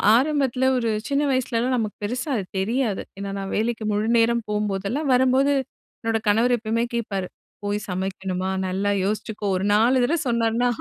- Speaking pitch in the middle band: No, high, 225 Hz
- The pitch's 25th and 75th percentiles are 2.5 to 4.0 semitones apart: Yes, average, 3.4 semitones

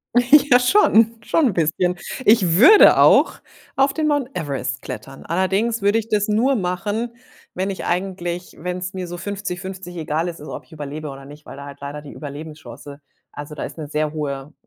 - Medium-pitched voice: Yes, medium, 180 Hz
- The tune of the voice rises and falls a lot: Yes, wide, 6.1 semitones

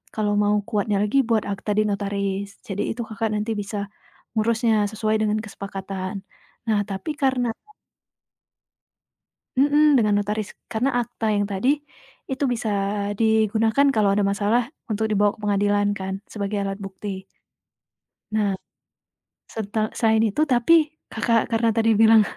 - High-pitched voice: Yes, high, 215 Hz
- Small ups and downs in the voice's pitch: Yes, narrow, 2.0 semitones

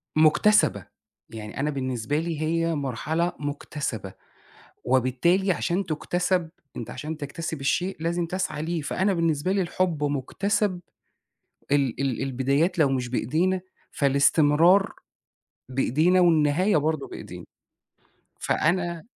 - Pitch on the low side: No, medium, 155 Hz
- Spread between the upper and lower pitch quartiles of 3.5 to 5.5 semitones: Yes, average, 4.1 semitones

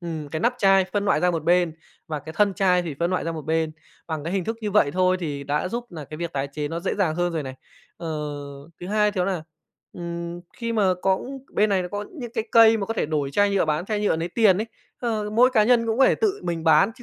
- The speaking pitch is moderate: Yes, medium, 180 Hz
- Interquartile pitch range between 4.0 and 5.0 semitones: Yes, average, 4.4 semitones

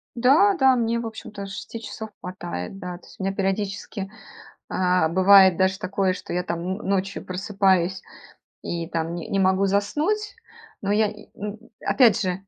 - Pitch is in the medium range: No, high, 195 Hz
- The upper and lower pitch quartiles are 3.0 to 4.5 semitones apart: No, narrow, 2.4 semitones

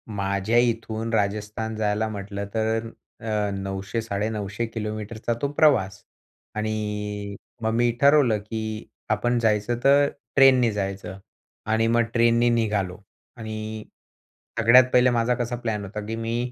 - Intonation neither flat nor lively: No, narrow, 2.1 semitones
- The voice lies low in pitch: Yes, low, 110 Hz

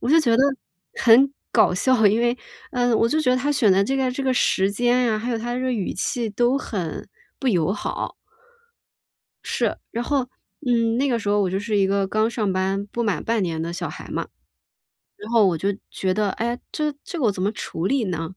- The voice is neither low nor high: No, high, 225 Hz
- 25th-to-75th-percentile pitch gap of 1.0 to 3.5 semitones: No, average, 4.1 semitones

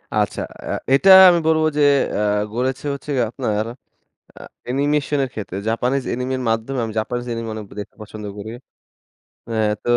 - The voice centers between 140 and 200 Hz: No, low, 125 Hz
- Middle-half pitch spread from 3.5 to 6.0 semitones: Yes, average, 3.9 semitones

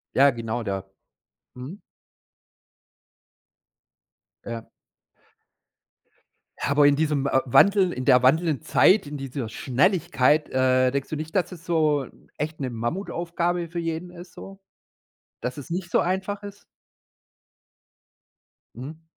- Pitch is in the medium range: Yes, medium, 150 Hz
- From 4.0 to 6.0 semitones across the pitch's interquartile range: Yes, average, 5.2 semitones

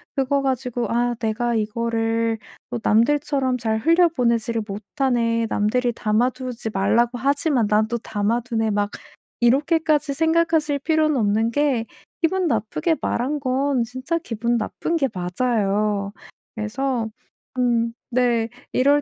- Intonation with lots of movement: No, average, 3.7 semitones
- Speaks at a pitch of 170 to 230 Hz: No, high, 240 Hz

